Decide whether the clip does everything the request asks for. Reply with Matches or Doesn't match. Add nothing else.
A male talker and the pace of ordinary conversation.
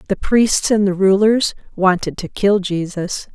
Doesn't match